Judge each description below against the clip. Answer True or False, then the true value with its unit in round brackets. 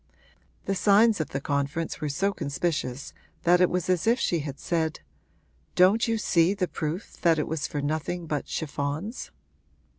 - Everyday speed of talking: True (170 wpm)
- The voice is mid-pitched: True (165 Hz)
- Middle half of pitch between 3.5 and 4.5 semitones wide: True (4.1 semitones)